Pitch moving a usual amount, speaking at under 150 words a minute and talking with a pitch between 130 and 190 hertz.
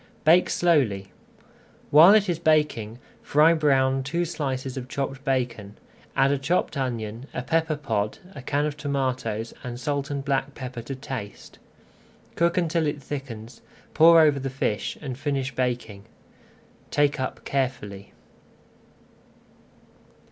Yes: average, 3.2 semitones; average, 140 wpm; low, 135 Hz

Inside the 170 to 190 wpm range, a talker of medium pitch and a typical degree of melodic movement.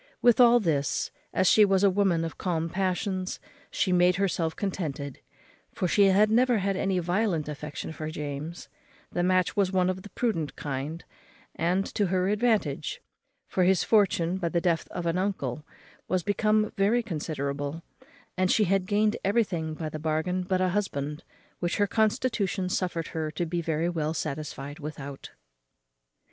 No: average, 160 wpm; medium, 180 Hz; average, 3.8 semitones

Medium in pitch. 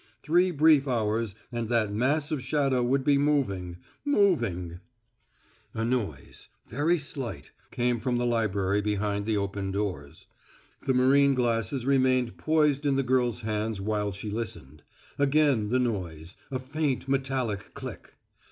No: low, 120 Hz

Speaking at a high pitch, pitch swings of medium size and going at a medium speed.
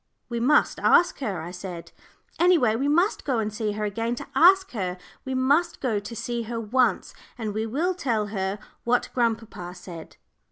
Yes: high, 230 Hz; average, 4.3 semitones; average, 190 wpm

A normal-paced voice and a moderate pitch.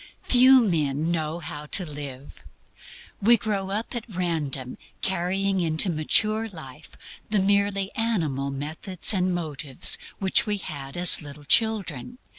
No: slow, 130 wpm; medium, 175 Hz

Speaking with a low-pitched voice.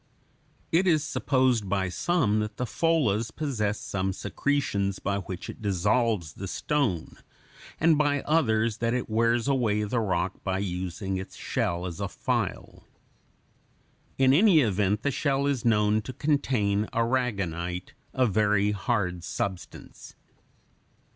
Yes: low, 110 Hz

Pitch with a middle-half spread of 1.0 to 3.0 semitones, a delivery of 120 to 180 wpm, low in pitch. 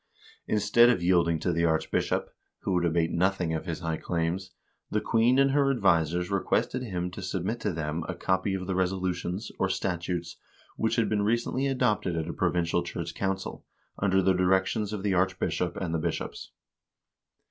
Yes: average, 2.7 semitones; average, 175 wpm; very low, 95 Hz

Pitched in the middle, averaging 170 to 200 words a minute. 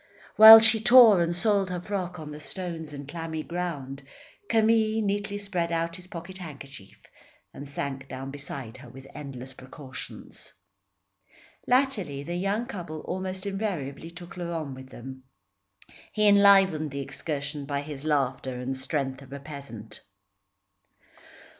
No: medium, 160 Hz; average, 140 wpm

